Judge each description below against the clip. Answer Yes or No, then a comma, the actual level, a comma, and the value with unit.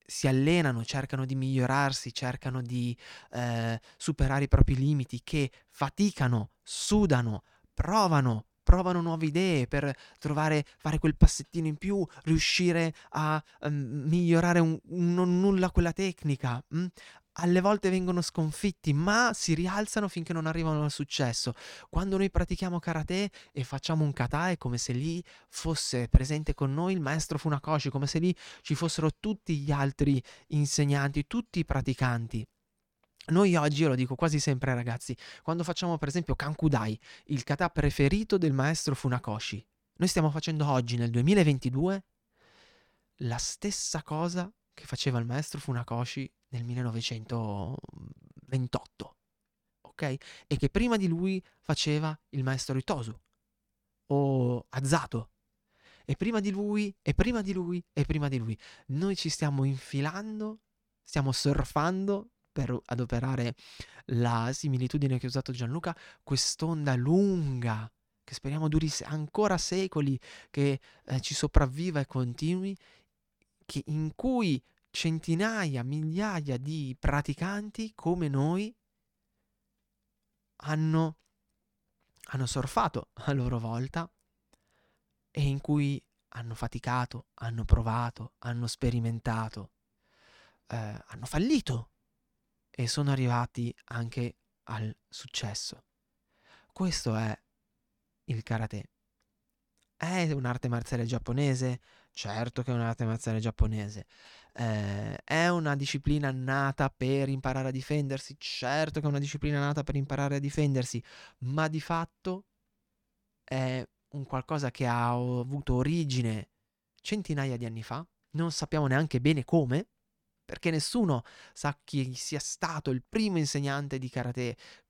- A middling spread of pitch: Yes, average, 4.6 semitones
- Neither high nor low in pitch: Yes, medium, 145 Hz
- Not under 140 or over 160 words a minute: No, average, 125 wpm